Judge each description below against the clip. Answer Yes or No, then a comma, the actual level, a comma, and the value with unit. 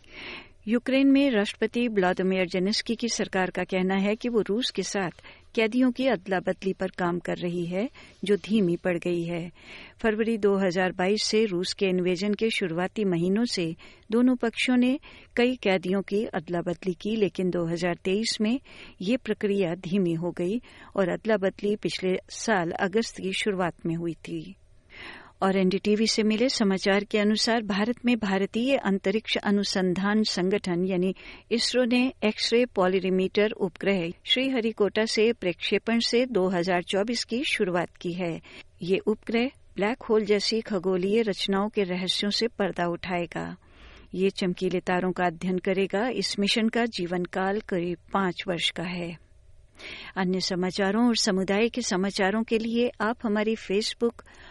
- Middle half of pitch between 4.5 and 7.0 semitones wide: No, average, 3.2 semitones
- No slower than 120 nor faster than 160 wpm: Yes, average, 150 wpm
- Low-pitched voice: No, high, 195 Hz